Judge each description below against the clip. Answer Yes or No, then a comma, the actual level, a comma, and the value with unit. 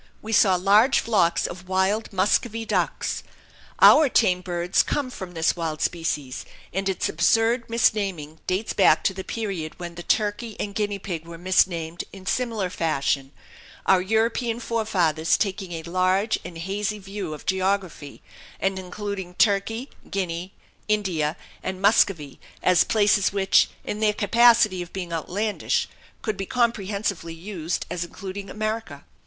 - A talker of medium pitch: No, high, 195 Hz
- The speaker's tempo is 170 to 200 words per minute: No, average, 145 wpm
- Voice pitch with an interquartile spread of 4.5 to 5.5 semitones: No, average, 3.5 semitones